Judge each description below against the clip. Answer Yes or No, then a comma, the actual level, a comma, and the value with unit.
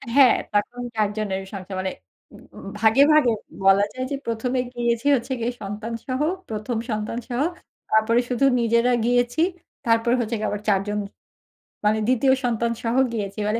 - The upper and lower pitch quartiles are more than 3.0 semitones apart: No, narrow, 2.4 semitones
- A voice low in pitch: No, high, 230 Hz